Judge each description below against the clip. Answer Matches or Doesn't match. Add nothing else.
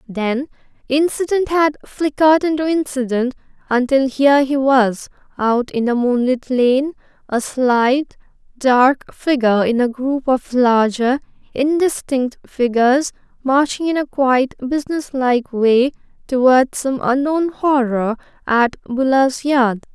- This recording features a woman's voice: Matches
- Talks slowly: Matches